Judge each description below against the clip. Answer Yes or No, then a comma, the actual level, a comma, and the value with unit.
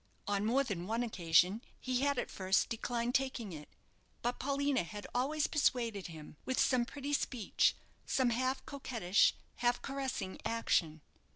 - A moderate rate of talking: Yes, average, 150 wpm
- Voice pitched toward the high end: Yes, high, 240 Hz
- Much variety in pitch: No, average, 4.8 semitones